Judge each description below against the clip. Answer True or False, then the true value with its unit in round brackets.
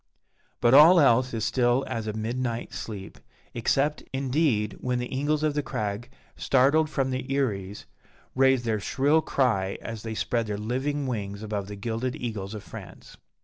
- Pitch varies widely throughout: False (3.9 semitones)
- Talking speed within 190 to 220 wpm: False (165 wpm)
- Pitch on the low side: True (120 Hz)